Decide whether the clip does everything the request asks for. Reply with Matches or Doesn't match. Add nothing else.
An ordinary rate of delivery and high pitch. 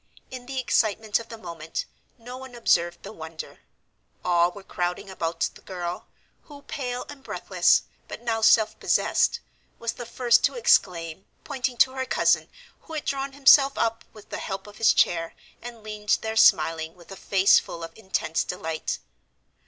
Matches